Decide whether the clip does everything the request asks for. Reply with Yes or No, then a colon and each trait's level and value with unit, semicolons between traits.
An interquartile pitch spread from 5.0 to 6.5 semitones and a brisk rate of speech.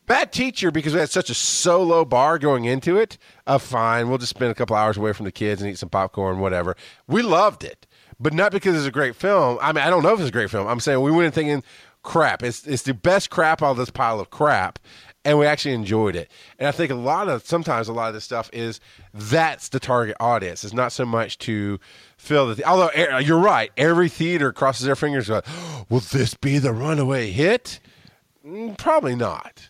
Yes: wide, 5.6 semitones; fast, 230 wpm